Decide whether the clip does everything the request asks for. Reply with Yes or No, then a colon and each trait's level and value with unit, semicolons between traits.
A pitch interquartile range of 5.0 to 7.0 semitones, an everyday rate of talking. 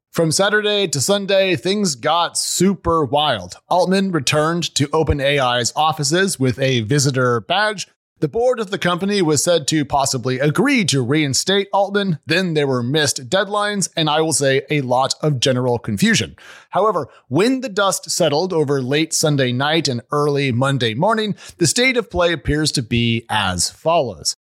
Yes: wide, 5.6 semitones; average, 160 wpm